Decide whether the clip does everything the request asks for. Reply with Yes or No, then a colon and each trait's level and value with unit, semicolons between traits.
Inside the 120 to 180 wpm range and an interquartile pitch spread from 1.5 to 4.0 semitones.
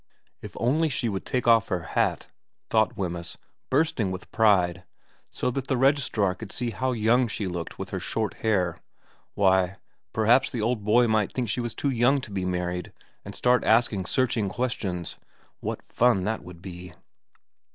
No: average, 170 wpm; average, 5.0 semitones